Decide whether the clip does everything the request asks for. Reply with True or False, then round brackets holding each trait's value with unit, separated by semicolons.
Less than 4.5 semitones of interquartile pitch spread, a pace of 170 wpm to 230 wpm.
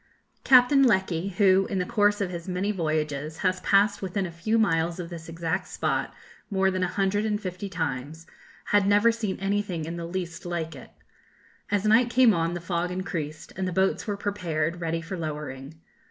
True (3.5 semitones; 190 wpm)